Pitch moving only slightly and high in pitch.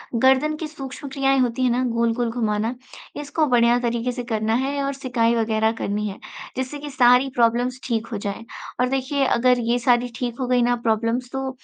Yes: narrow, 2.2 semitones; high, 245 Hz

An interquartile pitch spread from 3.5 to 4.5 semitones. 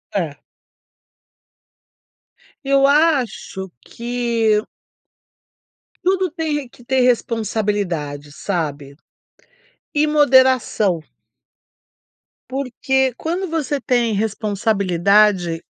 No: wide, 5.5 semitones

